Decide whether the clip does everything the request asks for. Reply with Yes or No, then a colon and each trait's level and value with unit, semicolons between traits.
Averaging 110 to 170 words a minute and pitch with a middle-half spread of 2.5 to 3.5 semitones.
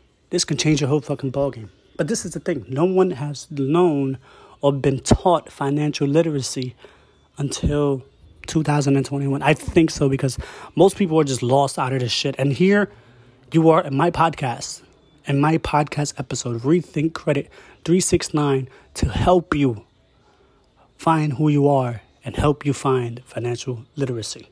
Yes: average, 155 wpm; average, 3.2 semitones